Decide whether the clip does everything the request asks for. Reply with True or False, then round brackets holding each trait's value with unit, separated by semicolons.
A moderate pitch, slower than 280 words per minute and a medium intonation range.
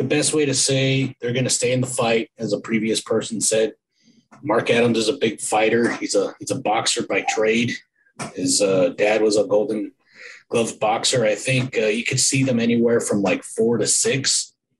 False (115 Hz; 205 wpm; 3.0 semitones)